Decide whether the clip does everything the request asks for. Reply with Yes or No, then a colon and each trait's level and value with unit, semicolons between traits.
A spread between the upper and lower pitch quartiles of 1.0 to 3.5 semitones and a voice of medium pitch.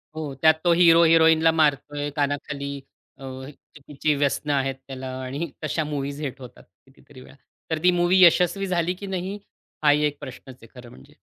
Yes: average, 3.0 semitones; medium, 150 Hz